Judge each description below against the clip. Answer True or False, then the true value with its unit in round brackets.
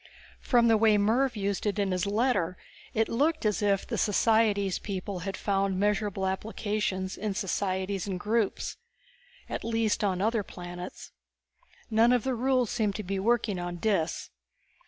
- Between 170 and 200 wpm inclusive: False (155 wpm)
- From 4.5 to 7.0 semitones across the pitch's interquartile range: False (2.8 semitones)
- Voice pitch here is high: True (205 Hz)